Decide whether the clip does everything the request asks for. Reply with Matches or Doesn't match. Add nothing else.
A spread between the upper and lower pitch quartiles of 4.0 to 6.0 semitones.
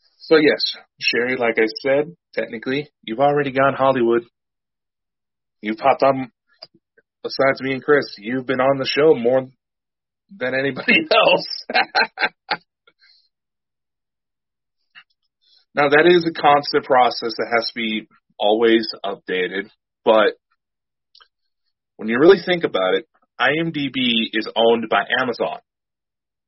Matches